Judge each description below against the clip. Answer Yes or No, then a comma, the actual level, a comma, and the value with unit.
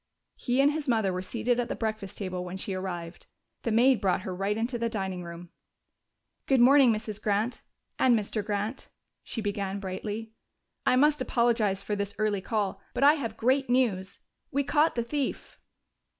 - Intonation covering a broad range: No, average, 4.1 semitones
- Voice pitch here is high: Yes, high, 220 Hz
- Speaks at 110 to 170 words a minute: No, average, 180 wpm